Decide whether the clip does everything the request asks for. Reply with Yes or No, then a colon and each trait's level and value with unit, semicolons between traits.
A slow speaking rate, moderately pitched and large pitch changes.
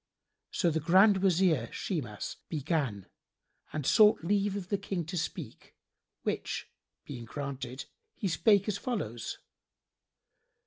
Yes: slow, 120 wpm; medium, 170 Hz; wide, 6.3 semitones